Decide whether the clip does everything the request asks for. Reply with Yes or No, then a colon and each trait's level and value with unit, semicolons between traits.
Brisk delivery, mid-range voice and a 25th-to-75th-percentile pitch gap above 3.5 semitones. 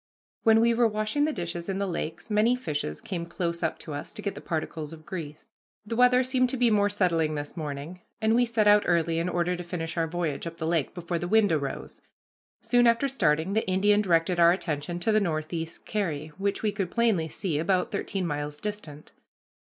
Yes: fast, 215 wpm; medium, 175 Hz; average, 4.6 semitones